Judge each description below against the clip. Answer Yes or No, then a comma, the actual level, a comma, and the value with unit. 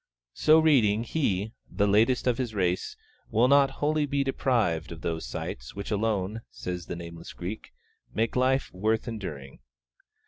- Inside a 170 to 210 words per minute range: No, average, 150 wpm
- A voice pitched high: No, low, 110 Hz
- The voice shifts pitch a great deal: Yes, wide, 6.2 semitones